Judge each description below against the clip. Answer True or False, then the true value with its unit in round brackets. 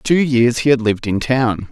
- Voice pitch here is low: True (125 Hz)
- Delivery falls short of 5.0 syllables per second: False (5.4 syllables/s)